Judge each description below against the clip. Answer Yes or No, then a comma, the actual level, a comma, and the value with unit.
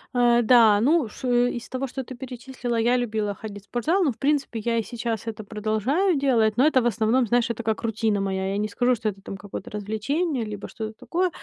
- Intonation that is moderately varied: Yes, average, 3.2 semitones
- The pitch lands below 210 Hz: No, high, 230 Hz